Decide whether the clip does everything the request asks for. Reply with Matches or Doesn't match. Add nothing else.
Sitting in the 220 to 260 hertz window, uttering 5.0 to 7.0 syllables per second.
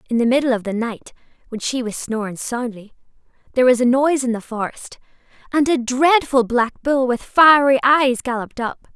Matches